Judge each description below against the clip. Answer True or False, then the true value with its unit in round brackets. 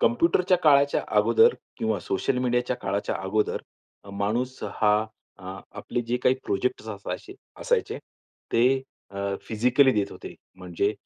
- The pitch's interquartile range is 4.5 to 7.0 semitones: True (4.8 semitones)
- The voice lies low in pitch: True (120 Hz)